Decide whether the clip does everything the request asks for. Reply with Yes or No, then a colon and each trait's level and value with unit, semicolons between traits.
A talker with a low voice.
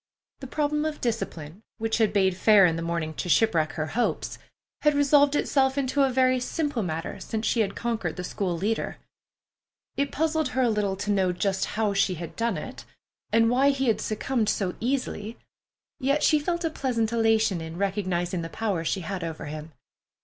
No: high, 220 Hz